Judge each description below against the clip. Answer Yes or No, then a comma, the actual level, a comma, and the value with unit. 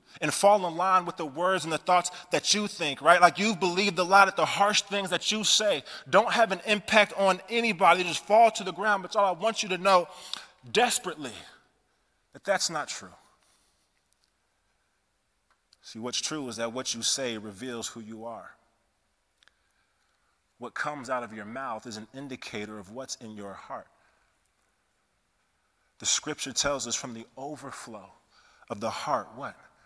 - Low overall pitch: No, medium, 170 Hz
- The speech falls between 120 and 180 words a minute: Yes, average, 175 wpm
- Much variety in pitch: Yes, wide, 9.0 semitones